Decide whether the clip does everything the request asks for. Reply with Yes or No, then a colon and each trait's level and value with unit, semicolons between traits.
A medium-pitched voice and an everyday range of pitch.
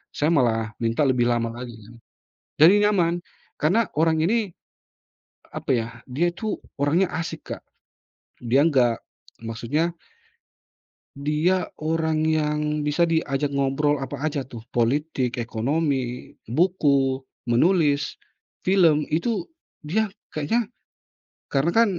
Yes: medium, 150 Hz; average, 4.7 semitones